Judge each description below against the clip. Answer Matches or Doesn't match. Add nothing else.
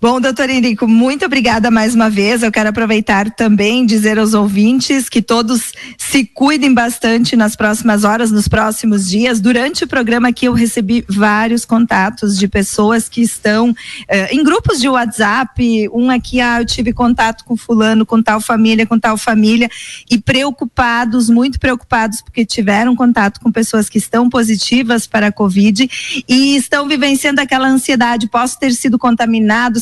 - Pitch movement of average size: Doesn't match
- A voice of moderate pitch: Doesn't match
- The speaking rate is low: Doesn't match